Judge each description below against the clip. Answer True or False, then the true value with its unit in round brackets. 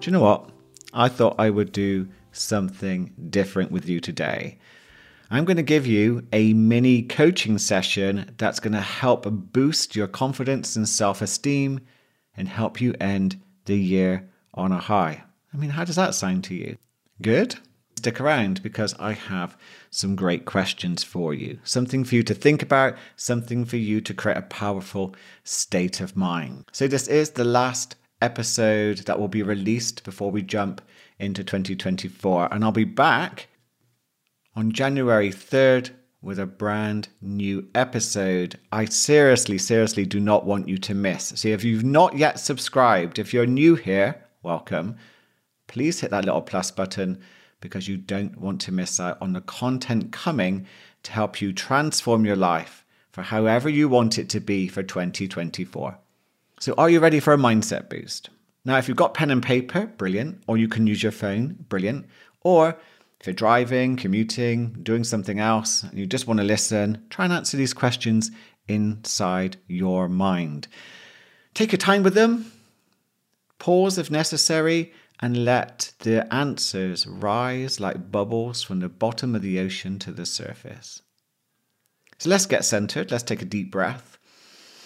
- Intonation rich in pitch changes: False (4.6 semitones)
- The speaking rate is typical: True (165 wpm)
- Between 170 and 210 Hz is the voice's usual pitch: False (110 Hz)